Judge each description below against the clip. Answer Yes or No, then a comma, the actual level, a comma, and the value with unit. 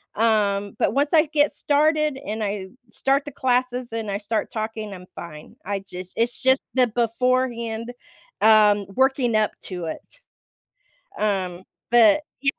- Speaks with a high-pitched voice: Yes, high, 225 Hz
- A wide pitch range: No, average, 4.2 semitones